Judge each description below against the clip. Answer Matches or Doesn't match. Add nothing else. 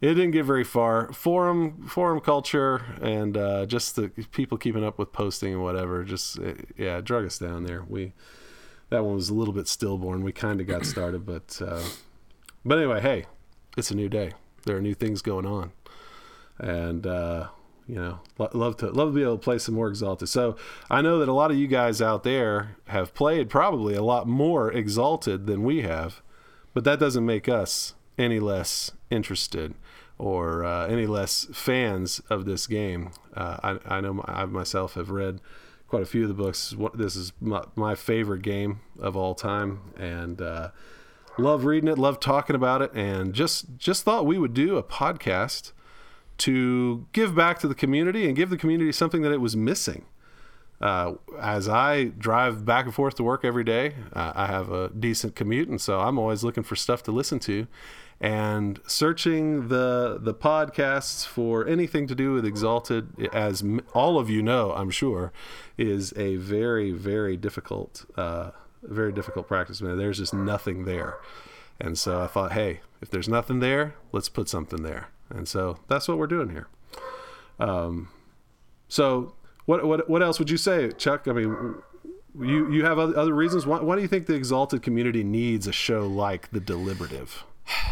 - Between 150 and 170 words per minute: Doesn't match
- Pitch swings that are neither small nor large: Doesn't match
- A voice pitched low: Matches